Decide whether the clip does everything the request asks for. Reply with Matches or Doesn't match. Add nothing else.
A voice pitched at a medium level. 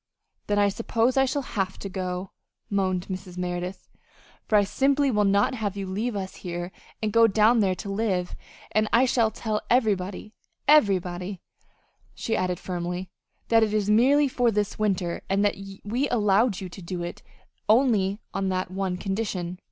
Doesn't match